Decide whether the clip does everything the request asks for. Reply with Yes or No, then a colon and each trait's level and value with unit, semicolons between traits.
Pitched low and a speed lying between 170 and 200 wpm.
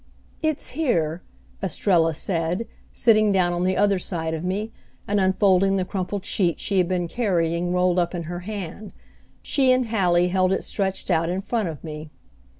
No: medium, 185 Hz; average, 175 wpm